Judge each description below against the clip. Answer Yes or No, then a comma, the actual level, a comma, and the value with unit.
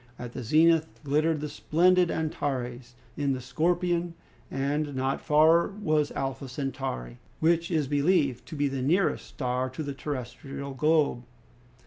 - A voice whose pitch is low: No, medium, 145 Hz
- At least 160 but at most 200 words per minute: No, average, 140 wpm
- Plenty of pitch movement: No, average, 3.4 semitones